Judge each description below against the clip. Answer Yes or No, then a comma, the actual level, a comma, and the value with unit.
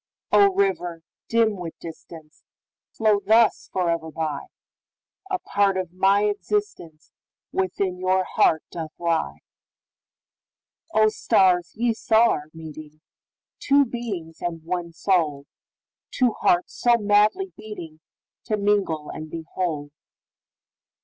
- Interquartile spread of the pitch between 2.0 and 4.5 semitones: No, average, 5.0 semitones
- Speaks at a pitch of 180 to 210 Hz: Yes, medium, 185 Hz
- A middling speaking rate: No, slow, 95 wpm